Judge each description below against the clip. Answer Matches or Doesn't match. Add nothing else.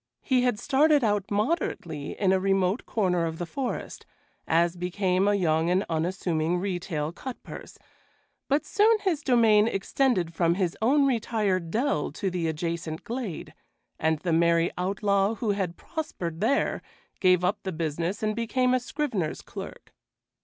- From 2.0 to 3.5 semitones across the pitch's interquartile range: Doesn't match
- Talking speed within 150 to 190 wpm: Matches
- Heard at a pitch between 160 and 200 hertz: Matches